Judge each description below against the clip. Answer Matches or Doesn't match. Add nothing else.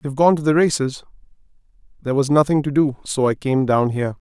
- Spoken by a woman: Doesn't match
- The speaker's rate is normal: Doesn't match